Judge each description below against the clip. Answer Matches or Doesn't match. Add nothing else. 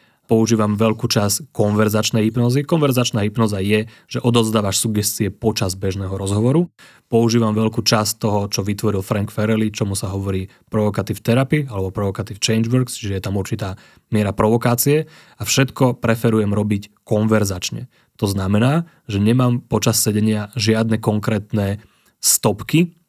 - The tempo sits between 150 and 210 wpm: Doesn't match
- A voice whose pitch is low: Matches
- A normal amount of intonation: Doesn't match